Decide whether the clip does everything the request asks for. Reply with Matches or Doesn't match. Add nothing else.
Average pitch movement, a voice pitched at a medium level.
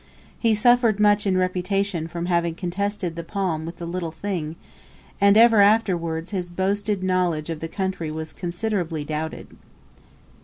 Matches